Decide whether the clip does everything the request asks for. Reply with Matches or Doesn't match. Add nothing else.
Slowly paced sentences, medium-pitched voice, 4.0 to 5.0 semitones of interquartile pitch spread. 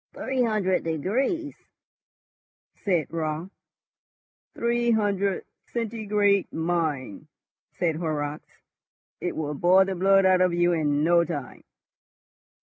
Matches